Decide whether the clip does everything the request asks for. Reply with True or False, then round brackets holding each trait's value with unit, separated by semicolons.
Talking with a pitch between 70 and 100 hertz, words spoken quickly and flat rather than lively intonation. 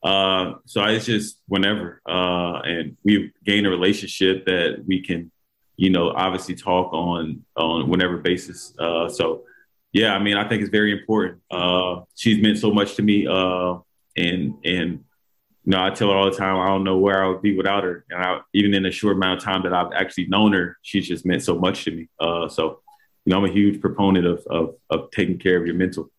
True (95 Hz; 220 wpm; 2.1 semitones)